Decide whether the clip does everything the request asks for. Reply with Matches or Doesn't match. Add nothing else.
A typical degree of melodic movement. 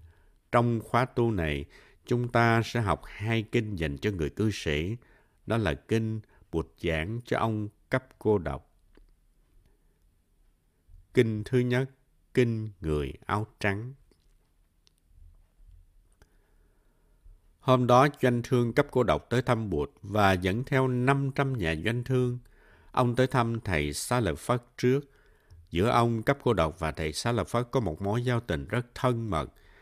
Doesn't match